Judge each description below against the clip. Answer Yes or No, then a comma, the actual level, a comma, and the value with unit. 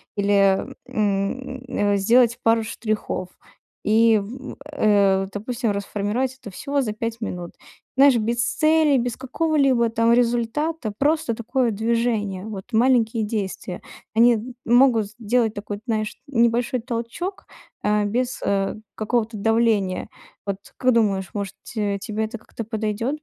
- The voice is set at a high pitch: Yes, high, 225 Hz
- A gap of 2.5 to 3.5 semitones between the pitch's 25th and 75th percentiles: Yes, average, 3.0 semitones